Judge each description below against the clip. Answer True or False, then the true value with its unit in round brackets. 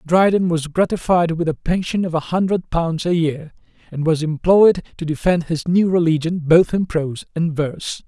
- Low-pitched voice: False (165 Hz)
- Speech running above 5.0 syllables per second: False (4.9 syllables/s)